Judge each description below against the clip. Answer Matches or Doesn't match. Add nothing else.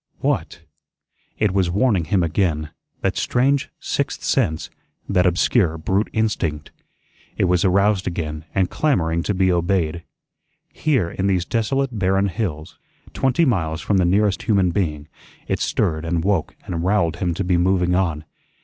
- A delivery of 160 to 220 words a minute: Doesn't match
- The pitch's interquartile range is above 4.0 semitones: Doesn't match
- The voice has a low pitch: Matches